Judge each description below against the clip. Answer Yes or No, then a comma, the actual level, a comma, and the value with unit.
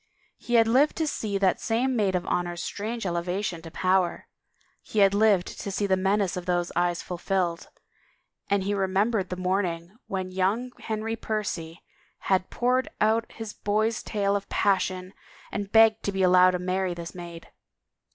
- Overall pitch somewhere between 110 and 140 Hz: No, high, 195 Hz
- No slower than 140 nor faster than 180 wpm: Yes, average, 170 wpm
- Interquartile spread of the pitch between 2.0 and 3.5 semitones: Yes, average, 3.0 semitones